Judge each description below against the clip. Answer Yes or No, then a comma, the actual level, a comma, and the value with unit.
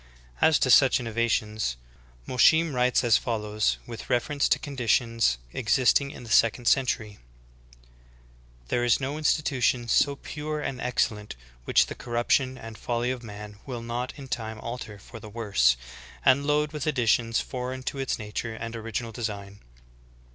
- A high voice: No, low, 120 Hz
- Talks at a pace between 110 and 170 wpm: Yes, average, 155 wpm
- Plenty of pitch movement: No, average, 2.9 semitones